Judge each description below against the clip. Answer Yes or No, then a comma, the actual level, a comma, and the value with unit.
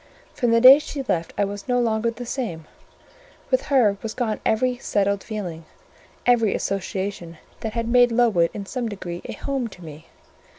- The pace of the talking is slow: No, average, 175 wpm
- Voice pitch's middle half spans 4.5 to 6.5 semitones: No, average, 3.8 semitones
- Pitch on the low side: No, high, 220 Hz